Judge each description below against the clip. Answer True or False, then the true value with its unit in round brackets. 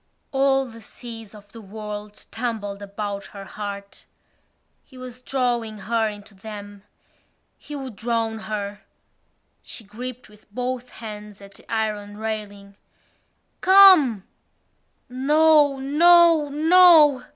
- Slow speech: True (115 wpm)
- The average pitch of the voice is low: False (225 Hz)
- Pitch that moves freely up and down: False (4.5 semitones)